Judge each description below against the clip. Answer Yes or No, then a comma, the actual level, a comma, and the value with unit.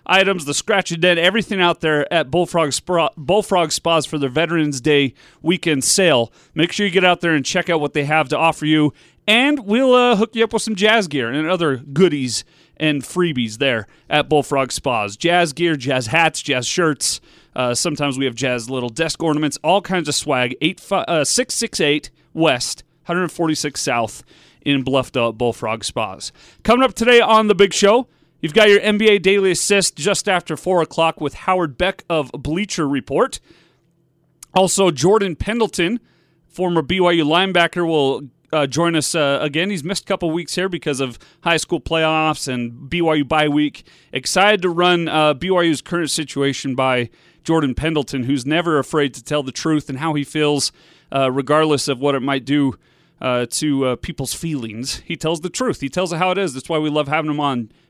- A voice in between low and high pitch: Yes, medium, 160 Hz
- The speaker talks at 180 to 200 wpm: Yes, average, 190 wpm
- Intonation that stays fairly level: No, average, 4.0 semitones